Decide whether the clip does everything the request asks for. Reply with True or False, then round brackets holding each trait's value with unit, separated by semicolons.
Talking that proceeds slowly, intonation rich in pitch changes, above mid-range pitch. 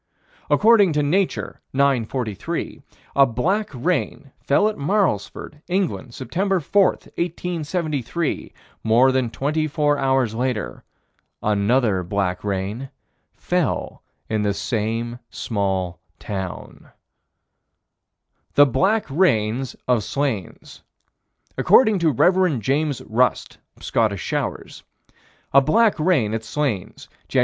False (105 wpm; 6.9 semitones; 135 Hz)